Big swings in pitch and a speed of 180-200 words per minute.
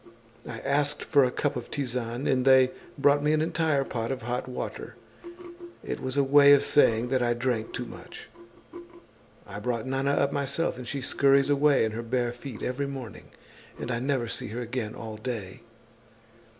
No: average, 2.9 semitones; average, 185 wpm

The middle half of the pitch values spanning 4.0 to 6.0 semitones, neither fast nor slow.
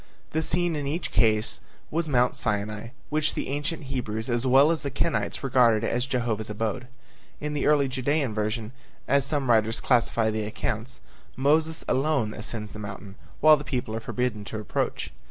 Yes: average, 4.7 semitones; average, 175 wpm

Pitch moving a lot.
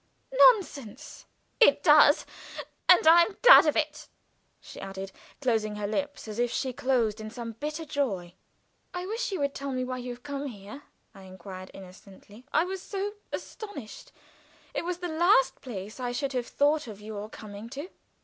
Yes: wide, 6.5 semitones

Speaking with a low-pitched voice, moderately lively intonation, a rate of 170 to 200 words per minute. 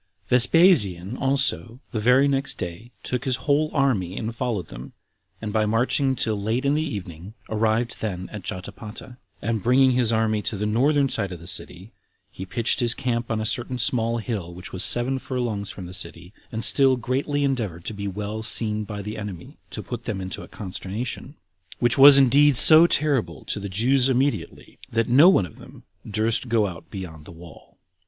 Yes: low, 115 Hz; average, 4.3 semitones; average, 190 wpm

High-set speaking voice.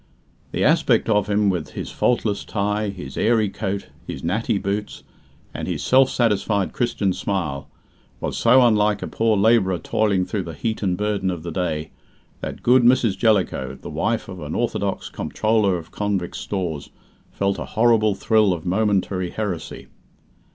No: low, 100 Hz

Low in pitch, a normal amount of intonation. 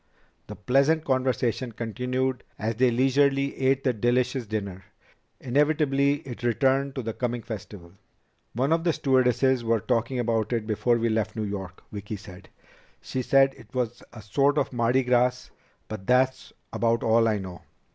Yes: low, 125 Hz; average, 3.0 semitones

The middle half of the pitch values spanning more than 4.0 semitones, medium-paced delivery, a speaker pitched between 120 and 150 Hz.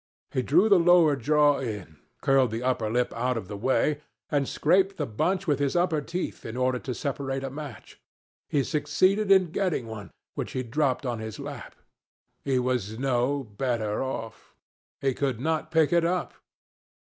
Yes: average, 4.4 semitones; average, 175 wpm; low, 135 Hz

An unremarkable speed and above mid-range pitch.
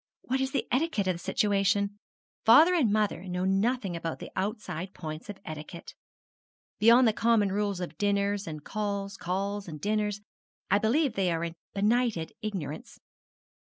Yes: average, 155 wpm; high, 200 Hz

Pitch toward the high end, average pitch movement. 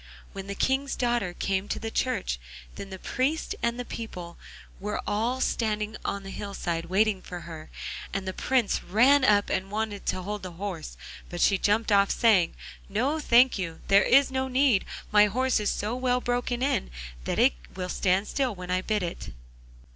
Yes: high, 210 Hz; average, 4.5 semitones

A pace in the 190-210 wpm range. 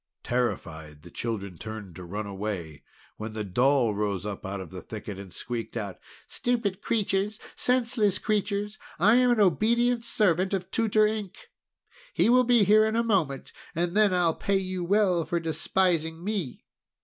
No: average, 165 wpm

